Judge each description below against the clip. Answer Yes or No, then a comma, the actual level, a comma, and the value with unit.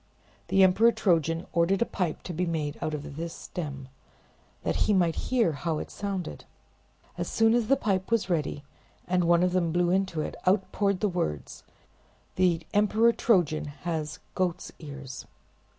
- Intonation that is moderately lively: Yes, average, 3.7 semitones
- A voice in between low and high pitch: Yes, medium, 175 Hz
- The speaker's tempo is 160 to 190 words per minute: Yes, average, 165 wpm